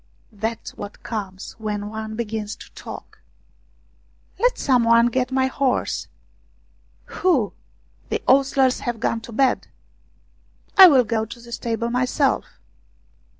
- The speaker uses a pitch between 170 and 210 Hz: No, high, 235 Hz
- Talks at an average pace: Yes, average, 145 wpm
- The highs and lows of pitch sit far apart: No, average, 3.1 semitones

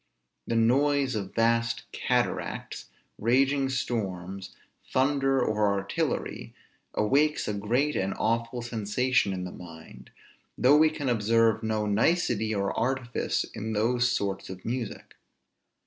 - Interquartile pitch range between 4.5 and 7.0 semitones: No, average, 3.9 semitones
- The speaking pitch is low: Yes, low, 115 Hz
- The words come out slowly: Yes, slow, 120 wpm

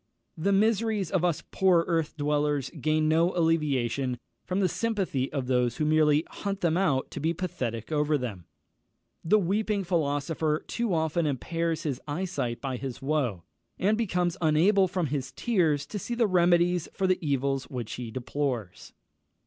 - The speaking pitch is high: No, medium, 155 Hz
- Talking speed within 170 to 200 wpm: No, average, 160 wpm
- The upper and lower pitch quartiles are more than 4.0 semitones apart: Yes, average, 4.7 semitones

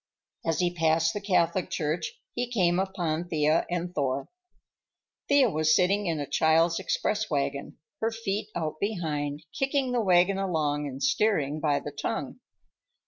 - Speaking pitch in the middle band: Yes, medium, 170 Hz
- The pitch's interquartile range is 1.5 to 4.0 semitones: No, average, 4.4 semitones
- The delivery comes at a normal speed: Yes, average, 150 wpm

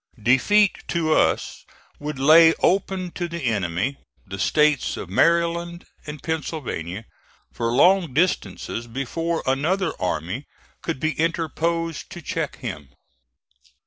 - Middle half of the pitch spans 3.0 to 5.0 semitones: No, wide, 5.5 semitones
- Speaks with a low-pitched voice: No, medium, 155 Hz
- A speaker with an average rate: No, slow, 115 wpm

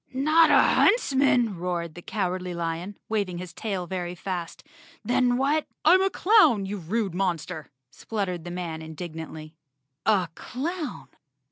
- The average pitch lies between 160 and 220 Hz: Yes, medium, 185 Hz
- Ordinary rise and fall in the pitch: No, wide, 6.2 semitones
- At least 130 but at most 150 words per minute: Yes, average, 140 wpm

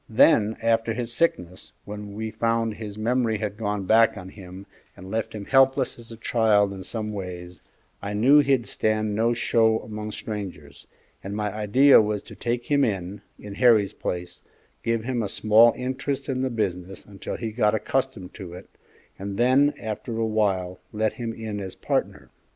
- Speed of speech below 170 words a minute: No, average, 180 wpm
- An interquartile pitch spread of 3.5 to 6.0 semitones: No, narrow, 2.5 semitones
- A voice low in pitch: Yes, low, 110 Hz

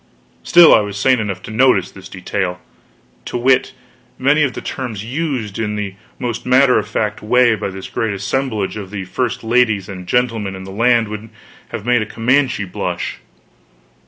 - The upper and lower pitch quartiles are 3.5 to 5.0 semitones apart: Yes, average, 3.9 semitones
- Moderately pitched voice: No, low, 110 Hz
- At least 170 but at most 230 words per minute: Yes, average, 180 wpm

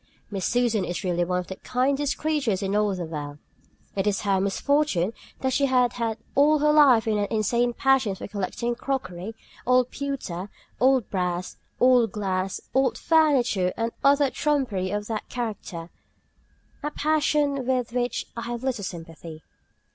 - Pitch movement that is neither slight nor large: No, wide, 5.9 semitones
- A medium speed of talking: Yes, average, 155 wpm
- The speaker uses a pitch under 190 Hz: No, high, 230 Hz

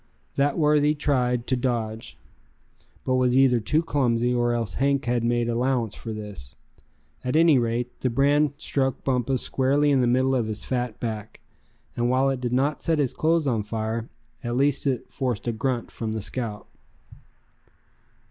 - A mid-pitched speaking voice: No, low, 125 Hz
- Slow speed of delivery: No, average, 170 wpm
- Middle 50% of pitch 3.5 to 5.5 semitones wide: No, average, 2.8 semitones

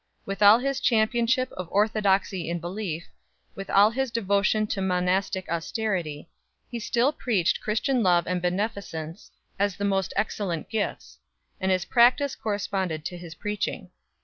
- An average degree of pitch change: Yes, average, 3.5 semitones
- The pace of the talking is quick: No, average, 145 wpm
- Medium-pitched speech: No, high, 200 Hz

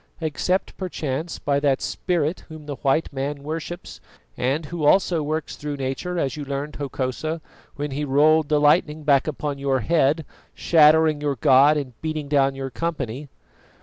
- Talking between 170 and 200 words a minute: No, average, 160 wpm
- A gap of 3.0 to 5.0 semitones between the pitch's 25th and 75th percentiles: No, narrow, 2.4 semitones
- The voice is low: No, medium, 150 Hz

